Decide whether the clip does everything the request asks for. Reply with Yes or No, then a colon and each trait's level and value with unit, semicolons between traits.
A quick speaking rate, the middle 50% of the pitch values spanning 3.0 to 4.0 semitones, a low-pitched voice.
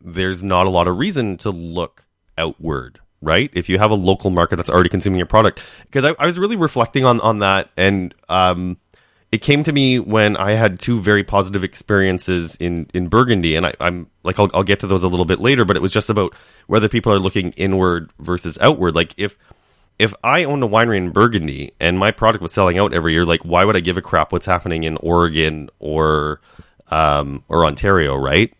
Yes: fast, 220 wpm; average, 3.6 semitones; very low, 95 Hz